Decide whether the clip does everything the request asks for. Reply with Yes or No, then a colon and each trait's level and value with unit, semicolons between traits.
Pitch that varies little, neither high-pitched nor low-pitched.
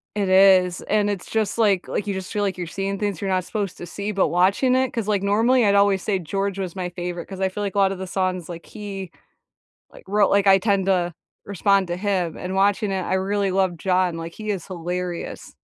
No: narrow, 1.9 semitones; high, 195 Hz